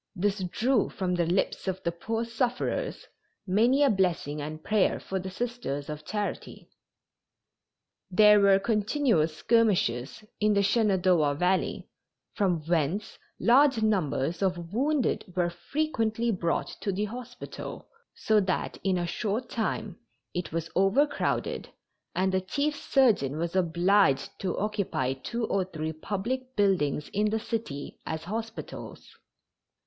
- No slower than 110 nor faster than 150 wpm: Yes, slow, 135 wpm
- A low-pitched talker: No, high, 195 Hz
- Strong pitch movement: No, average, 4.8 semitones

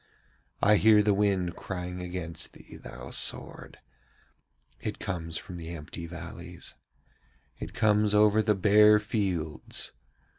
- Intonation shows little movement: No, average, 3.4 semitones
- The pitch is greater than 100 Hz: No, very low, 95 Hz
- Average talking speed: No, slow, 120 wpm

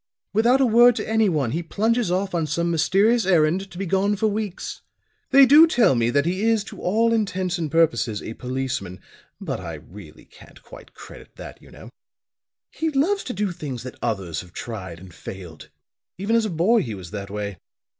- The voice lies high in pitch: No, medium, 175 Hz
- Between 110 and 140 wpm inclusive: No, average, 195 wpm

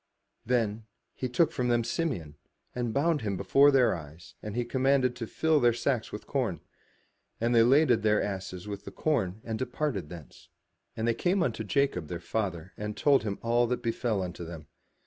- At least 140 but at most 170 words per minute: No, average, 185 wpm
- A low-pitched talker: Yes, low, 115 Hz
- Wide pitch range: No, average, 4.6 semitones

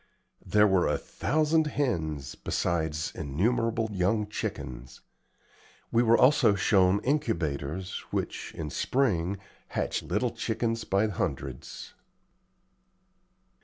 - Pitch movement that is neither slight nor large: No, wide, 6.4 semitones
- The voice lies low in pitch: Yes, low, 100 Hz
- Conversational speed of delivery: No, slow, 95 wpm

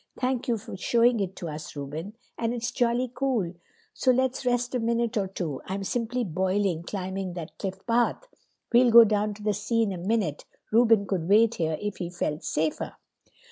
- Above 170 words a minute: Yes, average, 190 wpm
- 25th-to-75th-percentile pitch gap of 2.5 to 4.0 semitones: No, average, 4.4 semitones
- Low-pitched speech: No, high, 210 Hz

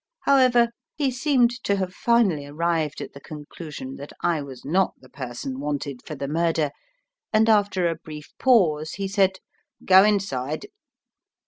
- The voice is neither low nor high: Yes, medium, 165 Hz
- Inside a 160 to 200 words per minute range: No, average, 150 wpm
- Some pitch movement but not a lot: No, wide, 5.9 semitones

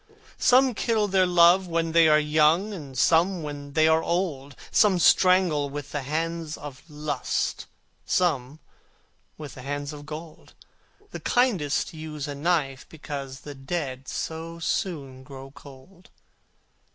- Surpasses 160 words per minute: No, average, 140 wpm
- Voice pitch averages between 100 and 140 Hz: No, medium, 155 Hz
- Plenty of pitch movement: No, average, 3.4 semitones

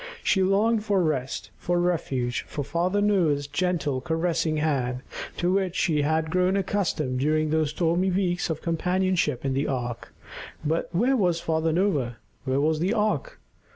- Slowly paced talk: No, average, 155 wpm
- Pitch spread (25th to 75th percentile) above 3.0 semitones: Yes, average, 4.1 semitones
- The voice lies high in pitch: No, medium, 165 Hz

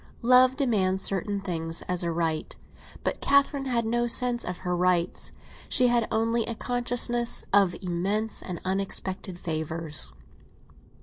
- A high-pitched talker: Yes, high, 200 Hz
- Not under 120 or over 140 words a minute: Yes, slow, 135 wpm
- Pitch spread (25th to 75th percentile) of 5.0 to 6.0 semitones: Yes, average, 5.3 semitones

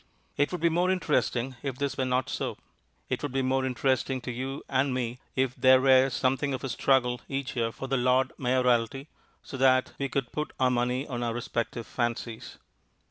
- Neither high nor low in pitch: No, low, 130 Hz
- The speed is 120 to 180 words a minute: No, average, 195 wpm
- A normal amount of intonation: No, narrow, 1.5 semitones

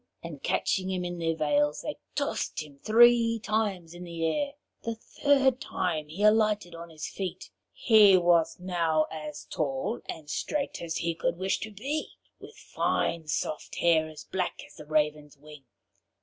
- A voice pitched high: No, medium, 170 Hz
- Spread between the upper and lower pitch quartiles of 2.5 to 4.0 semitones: No, wide, 5.4 semitones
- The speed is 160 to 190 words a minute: Yes, average, 165 wpm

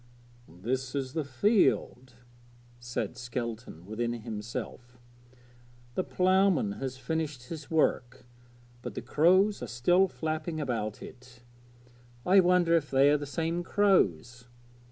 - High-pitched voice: No, low, 130 Hz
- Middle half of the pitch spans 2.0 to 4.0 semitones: No, wide, 5.6 semitones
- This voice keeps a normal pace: No, slow, 120 wpm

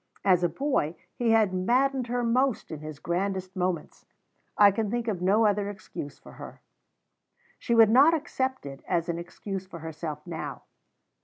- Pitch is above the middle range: Yes, high, 195 Hz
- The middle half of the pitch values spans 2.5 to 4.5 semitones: No, wide, 5.5 semitones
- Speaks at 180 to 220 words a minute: No, average, 170 wpm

